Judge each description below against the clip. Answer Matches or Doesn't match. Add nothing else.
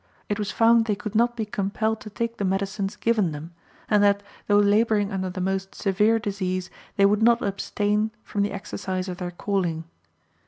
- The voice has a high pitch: Matches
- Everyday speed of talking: Matches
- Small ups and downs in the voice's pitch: Matches